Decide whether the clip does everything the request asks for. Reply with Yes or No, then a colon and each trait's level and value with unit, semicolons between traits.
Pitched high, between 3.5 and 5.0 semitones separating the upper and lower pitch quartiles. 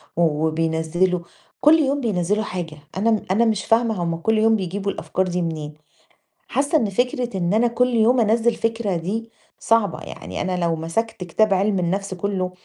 Yes: high, 200 Hz; average, 4.6 semitones